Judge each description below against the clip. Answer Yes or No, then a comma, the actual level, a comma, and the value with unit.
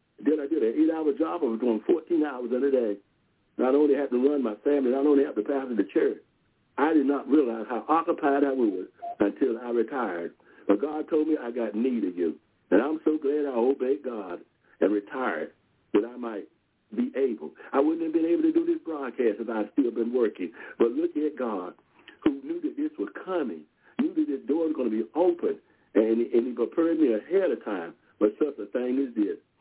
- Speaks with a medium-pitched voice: Yes, medium, 145 Hz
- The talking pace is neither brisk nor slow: No, fast, 225 wpm